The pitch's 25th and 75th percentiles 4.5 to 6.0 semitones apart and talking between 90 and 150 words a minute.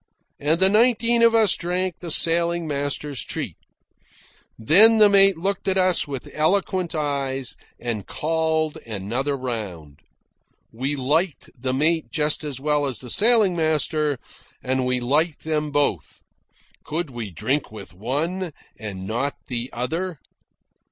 Yes: average, 5.3 semitones; average, 140 wpm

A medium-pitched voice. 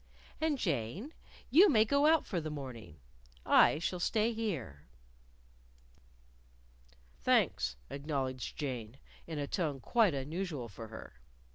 Yes: medium, 150 Hz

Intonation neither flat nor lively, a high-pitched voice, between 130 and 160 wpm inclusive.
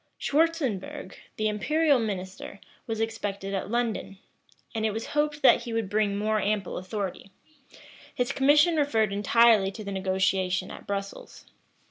Yes: average, 3.5 semitones; high, 215 Hz; average, 140 wpm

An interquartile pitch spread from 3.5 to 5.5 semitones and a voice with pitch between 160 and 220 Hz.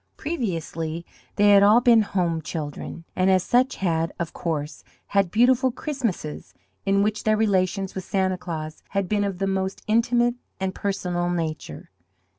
Yes: average, 4.0 semitones; high, 190 Hz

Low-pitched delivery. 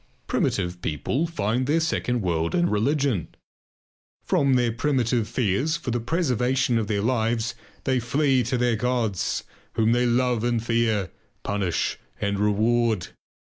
Yes: low, 120 Hz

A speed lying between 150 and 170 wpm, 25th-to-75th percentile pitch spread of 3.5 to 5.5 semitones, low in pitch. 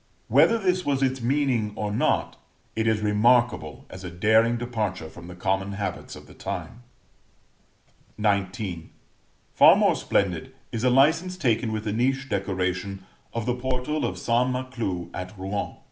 Yes: average, 155 wpm; average, 4.7 semitones; low, 110 Hz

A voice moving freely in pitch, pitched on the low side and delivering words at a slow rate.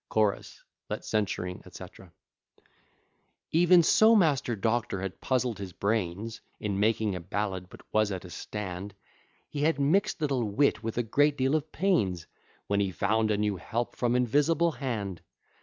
No: wide, 6.0 semitones; low, 110 Hz; average, 160 wpm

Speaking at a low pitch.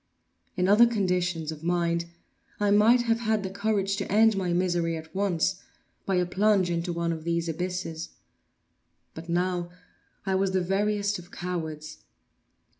No: medium, 180 Hz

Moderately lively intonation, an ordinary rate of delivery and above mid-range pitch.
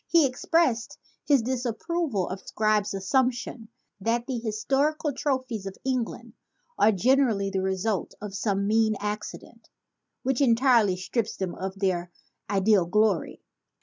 No: average, 4.7 semitones; slow, 125 wpm; high, 220 Hz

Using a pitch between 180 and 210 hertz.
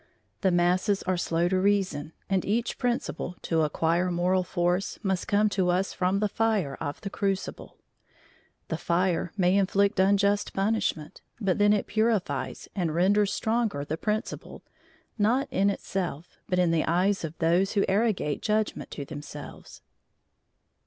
Yes: high, 190 Hz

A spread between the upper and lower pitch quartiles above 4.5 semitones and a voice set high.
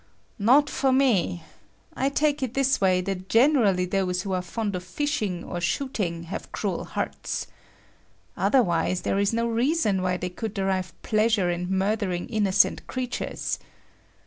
Yes: average, 5.3 semitones; high, 200 Hz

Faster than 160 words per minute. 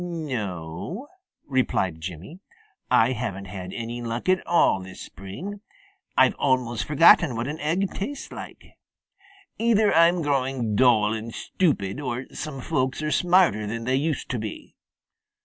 No: average, 140 wpm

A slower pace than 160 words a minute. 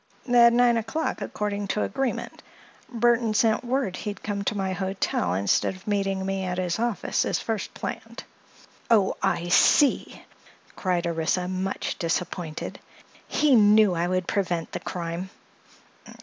Yes: average, 140 wpm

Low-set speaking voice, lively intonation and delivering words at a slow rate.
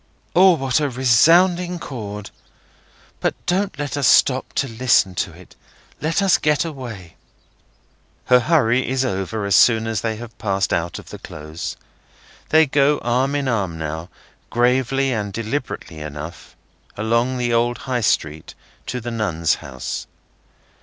No: low, 120 Hz; wide, 5.7 semitones; average, 145 wpm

